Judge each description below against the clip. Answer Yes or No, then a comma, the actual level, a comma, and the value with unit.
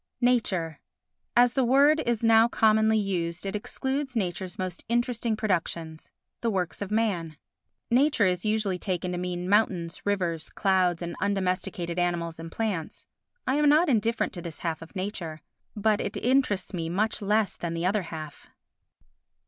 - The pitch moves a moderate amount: Yes, average, 4.4 semitones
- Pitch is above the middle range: Yes, high, 195 Hz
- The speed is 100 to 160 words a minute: Yes, average, 155 wpm